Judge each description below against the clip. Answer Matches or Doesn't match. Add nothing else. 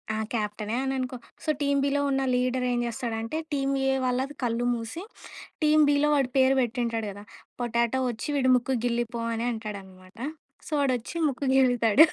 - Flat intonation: Doesn't match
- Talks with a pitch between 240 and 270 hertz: Matches